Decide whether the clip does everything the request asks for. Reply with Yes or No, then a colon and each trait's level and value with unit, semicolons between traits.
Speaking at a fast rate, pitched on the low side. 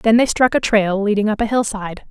No: fast, 255 wpm; high, 215 Hz